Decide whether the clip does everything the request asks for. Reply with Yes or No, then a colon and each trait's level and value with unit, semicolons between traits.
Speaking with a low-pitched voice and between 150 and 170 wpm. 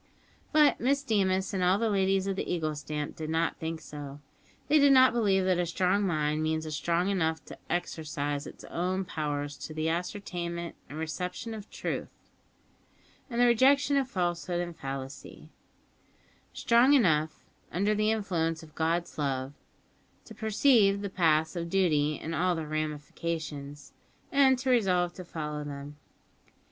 No: medium, 175 Hz; average, 160 wpm